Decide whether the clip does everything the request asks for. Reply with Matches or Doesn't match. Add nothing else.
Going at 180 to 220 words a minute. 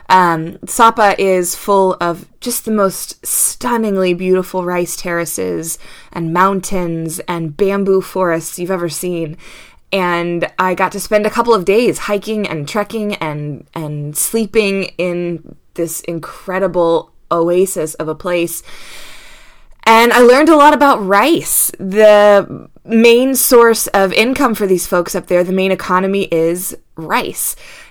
Doesn't match